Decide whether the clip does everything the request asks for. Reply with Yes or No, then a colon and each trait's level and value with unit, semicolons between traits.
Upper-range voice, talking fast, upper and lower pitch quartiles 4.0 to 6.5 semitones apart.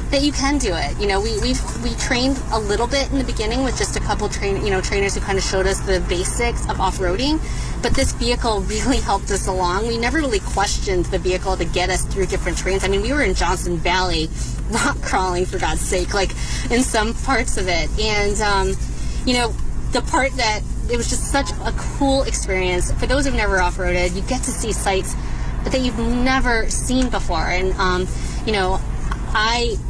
Yes: high, 195 Hz; fast, 215 wpm; average, 4.8 semitones